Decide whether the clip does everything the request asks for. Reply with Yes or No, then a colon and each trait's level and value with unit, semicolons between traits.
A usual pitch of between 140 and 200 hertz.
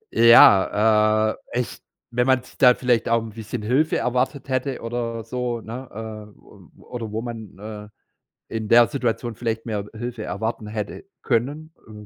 No: low, 115 Hz